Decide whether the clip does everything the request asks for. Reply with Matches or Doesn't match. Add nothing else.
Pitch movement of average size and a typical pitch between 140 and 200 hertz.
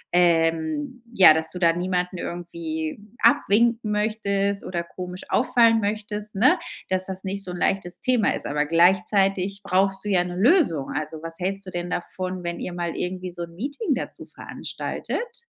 Matches